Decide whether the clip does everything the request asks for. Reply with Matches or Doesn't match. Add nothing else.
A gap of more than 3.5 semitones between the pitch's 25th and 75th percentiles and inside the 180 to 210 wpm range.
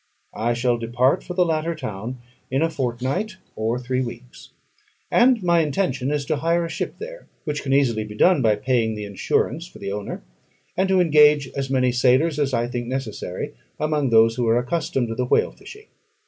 Matches